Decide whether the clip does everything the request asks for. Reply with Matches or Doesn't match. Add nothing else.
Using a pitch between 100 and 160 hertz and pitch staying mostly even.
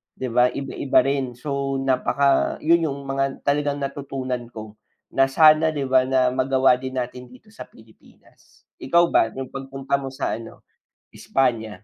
Matches